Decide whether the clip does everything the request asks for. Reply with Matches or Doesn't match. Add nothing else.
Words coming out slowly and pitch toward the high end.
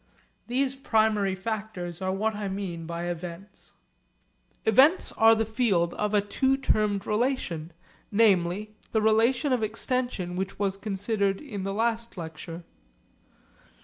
Matches